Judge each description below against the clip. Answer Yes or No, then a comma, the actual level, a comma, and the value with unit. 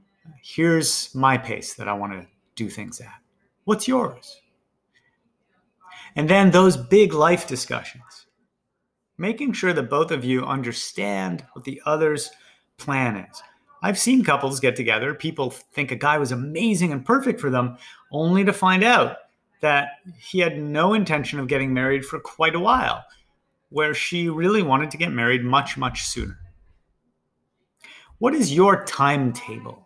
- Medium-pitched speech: Yes, medium, 150 Hz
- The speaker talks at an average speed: Yes, average, 150 wpm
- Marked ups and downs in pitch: Yes, wide, 6.5 semitones